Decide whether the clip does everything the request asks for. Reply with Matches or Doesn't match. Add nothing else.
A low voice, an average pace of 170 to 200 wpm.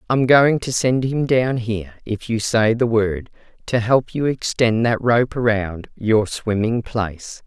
Matches